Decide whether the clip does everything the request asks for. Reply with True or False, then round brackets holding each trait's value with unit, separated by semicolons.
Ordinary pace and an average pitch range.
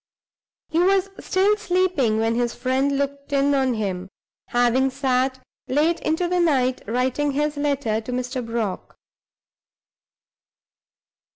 False (120 wpm; 3.5 semitones)